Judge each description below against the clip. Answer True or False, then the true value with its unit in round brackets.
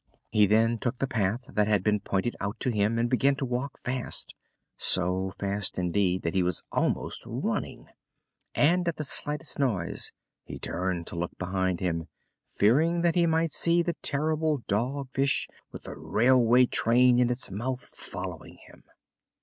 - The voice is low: True (120 Hz)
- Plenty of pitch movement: True (5.9 semitones)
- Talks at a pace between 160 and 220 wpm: True (165 wpm)